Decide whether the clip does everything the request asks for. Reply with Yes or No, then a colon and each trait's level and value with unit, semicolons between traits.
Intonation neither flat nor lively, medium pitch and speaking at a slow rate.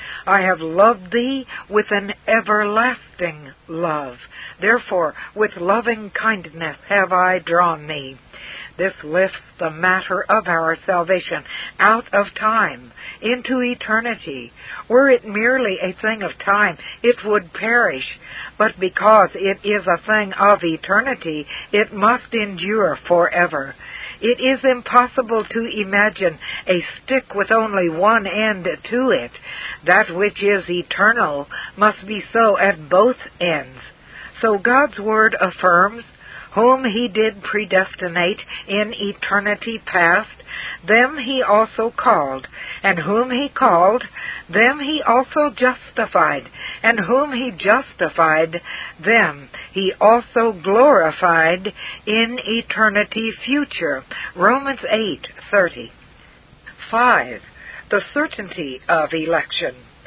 No: average, 4.0 semitones; high, 210 Hz; slow, 115 wpm